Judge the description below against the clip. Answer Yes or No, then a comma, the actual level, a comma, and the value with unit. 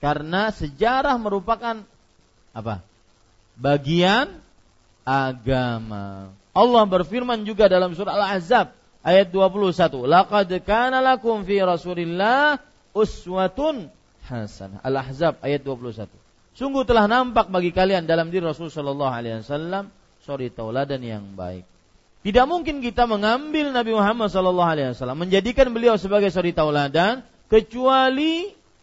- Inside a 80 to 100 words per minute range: No, average, 110 wpm